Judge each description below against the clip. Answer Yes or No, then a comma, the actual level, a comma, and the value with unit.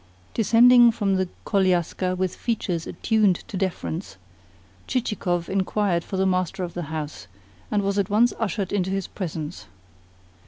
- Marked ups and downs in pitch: No, average, 2.9 semitones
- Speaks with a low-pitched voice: No, high, 190 Hz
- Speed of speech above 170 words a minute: No, average, 145 wpm